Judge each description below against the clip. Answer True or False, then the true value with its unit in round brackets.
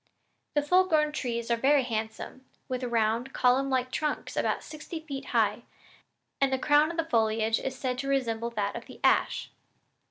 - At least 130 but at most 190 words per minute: True (170 wpm)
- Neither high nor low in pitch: False (255 Hz)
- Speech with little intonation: False (4.0 semitones)